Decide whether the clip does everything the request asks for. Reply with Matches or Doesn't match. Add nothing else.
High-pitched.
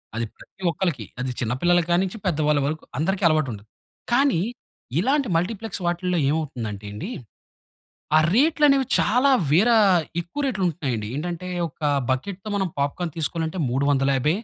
Doesn't match